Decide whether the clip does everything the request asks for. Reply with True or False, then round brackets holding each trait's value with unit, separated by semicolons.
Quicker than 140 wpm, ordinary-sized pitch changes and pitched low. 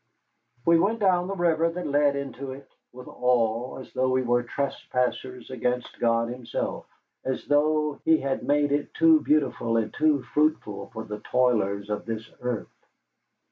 True (160 wpm; 4.2 semitones; 130 Hz)